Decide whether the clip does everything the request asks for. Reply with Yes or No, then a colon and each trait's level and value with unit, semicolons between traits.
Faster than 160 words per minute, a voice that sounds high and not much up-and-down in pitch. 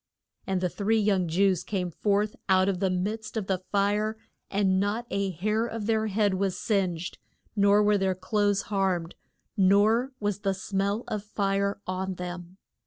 Yes: average, 175 wpm; high, 200 Hz; narrow, 1.9 semitones